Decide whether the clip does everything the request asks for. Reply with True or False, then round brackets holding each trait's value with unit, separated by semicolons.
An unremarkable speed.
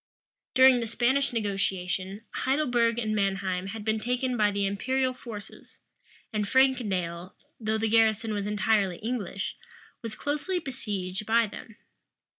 False (130 wpm)